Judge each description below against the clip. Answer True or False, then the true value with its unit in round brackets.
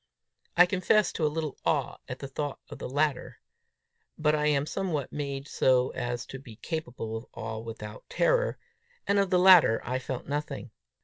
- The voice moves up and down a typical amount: True (4.4 semitones)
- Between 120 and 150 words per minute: False (180 wpm)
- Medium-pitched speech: True (145 Hz)